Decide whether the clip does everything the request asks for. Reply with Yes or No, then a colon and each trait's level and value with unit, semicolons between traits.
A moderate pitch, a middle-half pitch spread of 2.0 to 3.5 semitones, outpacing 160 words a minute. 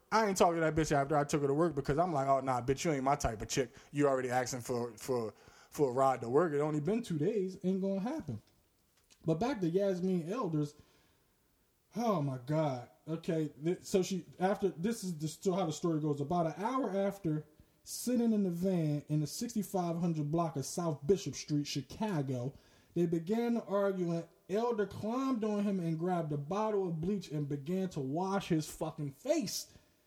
No: medium, 165 Hz; average, 5.1 semitones; average, 200 wpm